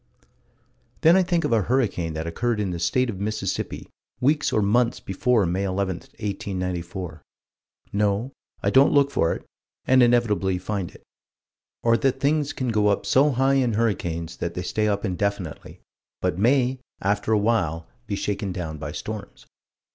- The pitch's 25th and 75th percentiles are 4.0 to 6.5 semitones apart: Yes, average, 5.2 semitones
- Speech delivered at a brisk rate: No, average, 165 wpm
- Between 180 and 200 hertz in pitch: No, low, 105 Hz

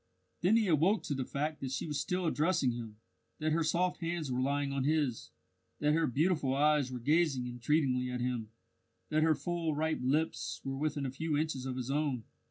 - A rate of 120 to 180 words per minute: No, average, 200 wpm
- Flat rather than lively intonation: No, average, 3.6 semitones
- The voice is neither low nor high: Yes, medium, 150 Hz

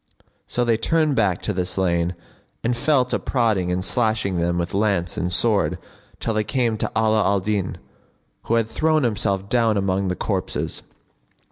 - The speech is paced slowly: No, average, 170 wpm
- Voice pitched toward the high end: No, low, 105 Hz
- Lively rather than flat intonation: No, average, 3.8 semitones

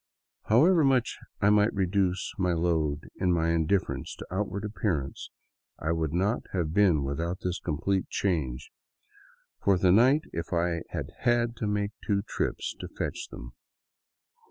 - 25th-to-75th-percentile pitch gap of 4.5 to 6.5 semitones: No, average, 3.9 semitones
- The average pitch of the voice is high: No, very low, 90 Hz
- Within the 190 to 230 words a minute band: No, average, 150 wpm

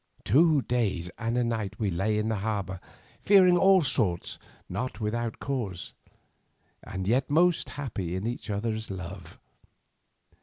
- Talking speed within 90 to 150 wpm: Yes, average, 140 wpm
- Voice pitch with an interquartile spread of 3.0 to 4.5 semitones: No, average, 5.0 semitones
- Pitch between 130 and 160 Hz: No, low, 110 Hz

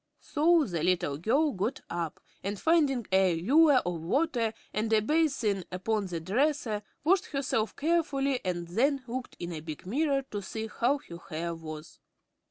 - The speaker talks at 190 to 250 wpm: No, average, 165 wpm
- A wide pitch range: Yes, wide, 7.9 semitones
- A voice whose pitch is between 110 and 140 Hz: No, high, 220 Hz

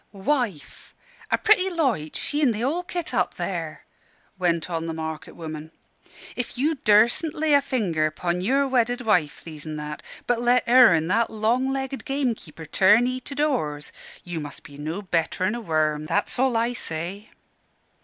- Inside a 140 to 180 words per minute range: Yes, average, 165 wpm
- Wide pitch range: Yes, wide, 8.2 semitones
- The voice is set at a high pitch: Yes, high, 215 Hz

